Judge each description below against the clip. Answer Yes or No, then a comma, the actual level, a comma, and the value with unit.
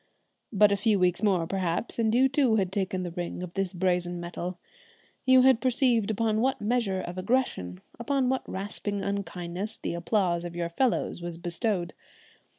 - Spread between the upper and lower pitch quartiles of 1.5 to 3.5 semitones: No, average, 4.4 semitones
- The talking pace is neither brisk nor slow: Yes, average, 170 wpm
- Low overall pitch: No, high, 195 Hz